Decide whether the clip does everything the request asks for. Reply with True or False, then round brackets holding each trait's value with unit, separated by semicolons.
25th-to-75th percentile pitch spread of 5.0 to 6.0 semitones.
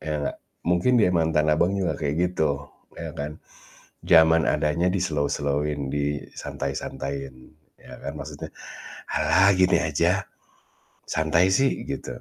False (3.5 semitones)